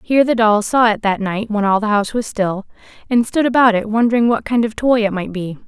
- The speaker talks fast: Yes, fast, 265 wpm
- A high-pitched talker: Yes, high, 220 Hz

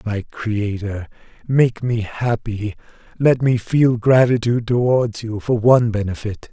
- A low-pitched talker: Yes, low, 115 Hz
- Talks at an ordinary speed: No, slow, 130 wpm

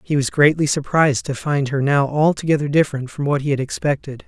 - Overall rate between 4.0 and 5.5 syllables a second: No, 6.0 syllables/s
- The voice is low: No, medium, 145 Hz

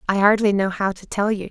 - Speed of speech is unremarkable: No, fast, 280 wpm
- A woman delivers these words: Yes, female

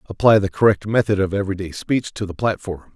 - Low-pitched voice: Yes, low, 100 Hz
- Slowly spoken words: No, fast, 205 wpm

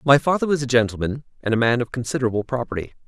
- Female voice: No, male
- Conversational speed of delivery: No, fast, 215 wpm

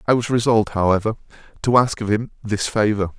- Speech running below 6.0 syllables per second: No, 6.1 syllables/s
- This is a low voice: Yes, low, 110 Hz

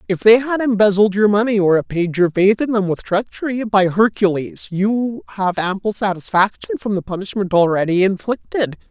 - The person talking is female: No, male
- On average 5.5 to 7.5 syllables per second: No, 5.1 syllables/s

